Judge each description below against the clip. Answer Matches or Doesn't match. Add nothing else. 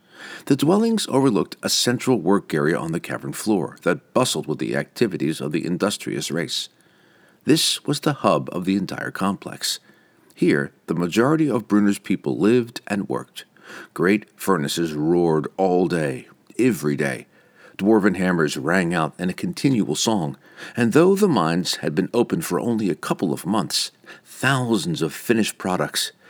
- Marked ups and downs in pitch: Matches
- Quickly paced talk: Doesn't match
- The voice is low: Matches